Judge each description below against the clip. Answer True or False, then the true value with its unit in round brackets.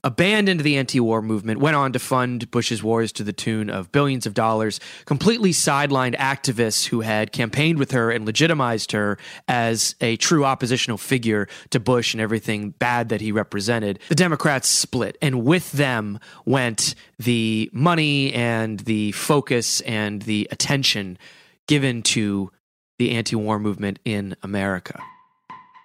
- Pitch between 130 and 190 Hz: False (120 Hz)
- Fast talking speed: False (145 wpm)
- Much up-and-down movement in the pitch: False (4.4 semitones)